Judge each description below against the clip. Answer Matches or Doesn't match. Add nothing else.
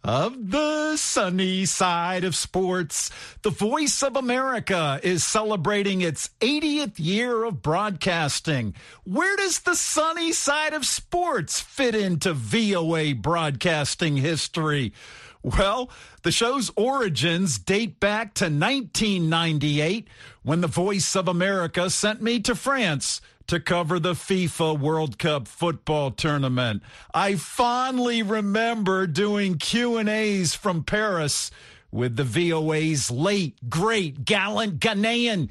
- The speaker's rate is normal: Doesn't match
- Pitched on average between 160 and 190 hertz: Matches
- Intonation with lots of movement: Matches